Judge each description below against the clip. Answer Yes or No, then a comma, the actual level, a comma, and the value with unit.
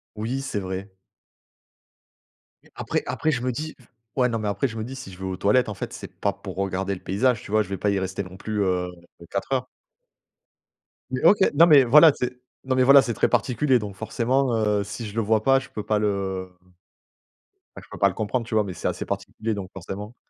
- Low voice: Yes, low, 110 Hz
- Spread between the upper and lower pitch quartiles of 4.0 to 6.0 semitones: Yes, average, 4.6 semitones